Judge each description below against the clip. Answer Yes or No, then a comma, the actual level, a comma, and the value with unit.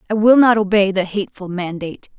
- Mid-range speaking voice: No, high, 200 Hz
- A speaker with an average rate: Yes, average, 190 wpm